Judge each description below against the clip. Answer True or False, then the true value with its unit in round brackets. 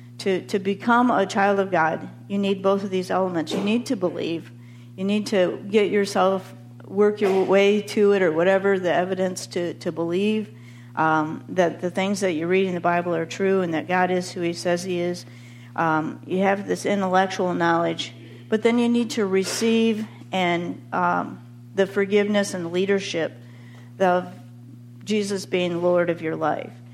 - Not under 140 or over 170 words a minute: False (180 wpm)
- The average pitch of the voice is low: False (180 Hz)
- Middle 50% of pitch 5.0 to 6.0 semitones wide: False (3.8 semitones)